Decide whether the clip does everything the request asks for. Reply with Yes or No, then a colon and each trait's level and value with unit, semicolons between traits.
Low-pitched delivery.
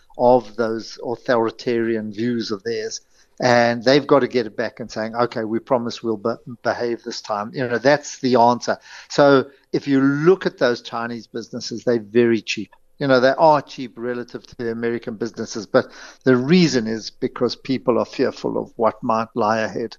Yes: low, 120 Hz